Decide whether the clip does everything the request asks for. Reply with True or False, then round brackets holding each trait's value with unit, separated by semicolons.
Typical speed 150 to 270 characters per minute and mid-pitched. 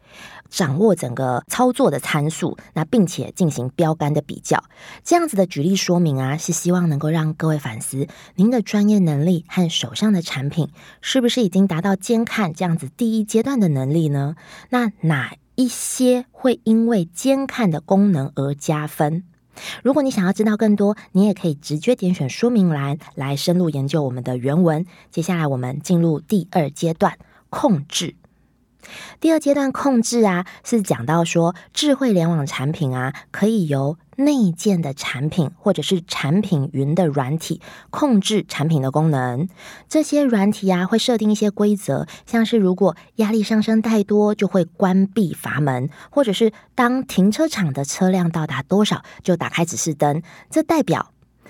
True (255 characters per minute; 180 Hz)